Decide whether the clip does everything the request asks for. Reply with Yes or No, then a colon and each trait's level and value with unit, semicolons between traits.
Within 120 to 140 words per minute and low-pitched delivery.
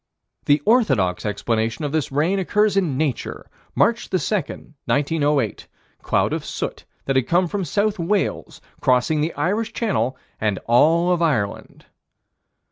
No: slow, 135 wpm; medium, 155 Hz